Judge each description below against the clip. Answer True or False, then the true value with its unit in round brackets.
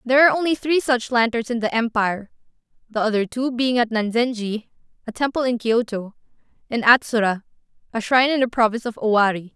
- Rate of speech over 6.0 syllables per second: True (6.2 syllables/s)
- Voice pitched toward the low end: False (235 Hz)